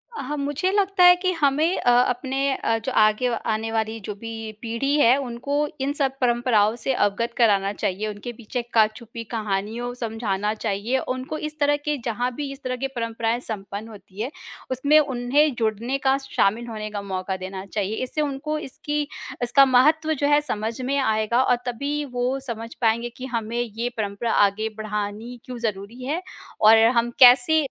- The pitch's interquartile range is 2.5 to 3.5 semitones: No, average, 3.9 semitones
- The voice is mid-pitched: No, high, 240 Hz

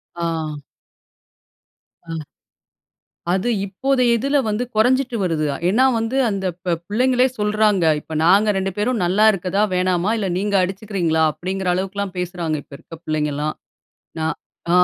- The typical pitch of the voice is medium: No, high, 195 Hz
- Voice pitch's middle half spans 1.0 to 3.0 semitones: No, average, 3.6 semitones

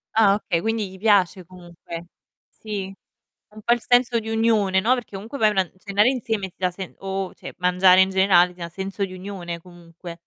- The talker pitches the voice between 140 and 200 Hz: Yes, high, 190 Hz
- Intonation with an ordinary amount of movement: Yes, average, 3.0 semitones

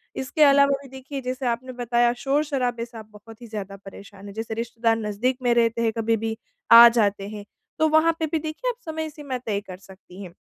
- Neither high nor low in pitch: No, high, 235 Hz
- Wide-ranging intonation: No, average, 3.9 semitones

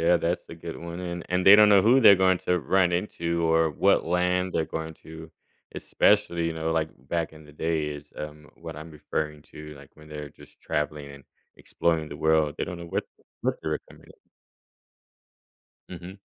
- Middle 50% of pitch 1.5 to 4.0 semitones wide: Yes, narrow, 2.5 semitones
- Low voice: Yes, very low, 80 Hz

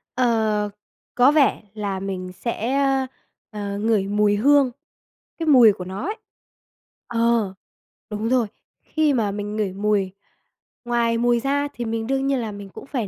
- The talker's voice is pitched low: No, high, 225 Hz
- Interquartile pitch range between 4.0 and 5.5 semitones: No, average, 3.6 semitones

